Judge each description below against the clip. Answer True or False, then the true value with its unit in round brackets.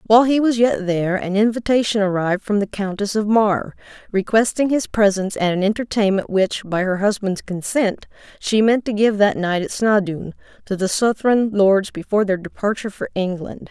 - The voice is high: True (205 Hz)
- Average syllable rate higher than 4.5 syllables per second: True (5.3 syllables/s)